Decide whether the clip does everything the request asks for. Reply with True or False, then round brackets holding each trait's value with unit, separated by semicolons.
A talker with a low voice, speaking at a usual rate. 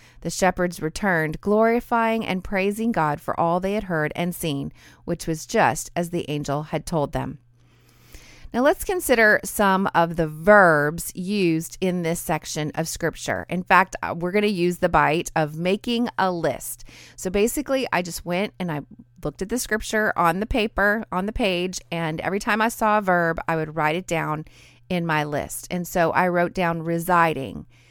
False (175 Hz; 185 wpm)